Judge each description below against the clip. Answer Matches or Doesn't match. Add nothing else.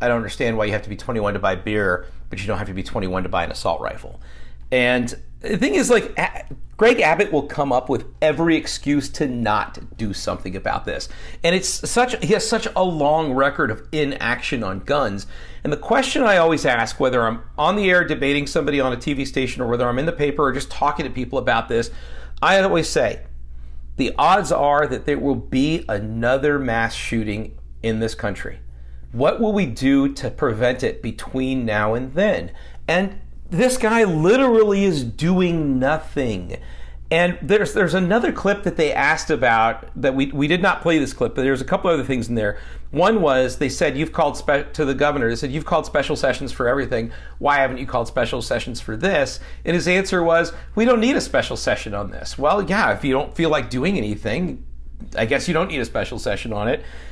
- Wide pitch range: Matches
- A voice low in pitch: Matches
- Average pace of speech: Doesn't match